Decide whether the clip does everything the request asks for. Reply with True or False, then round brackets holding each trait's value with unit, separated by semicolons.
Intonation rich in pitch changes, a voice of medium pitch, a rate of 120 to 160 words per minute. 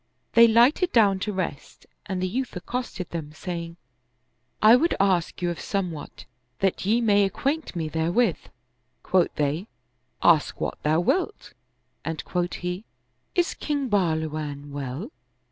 True (5.8 semitones; 180 Hz; 145 wpm)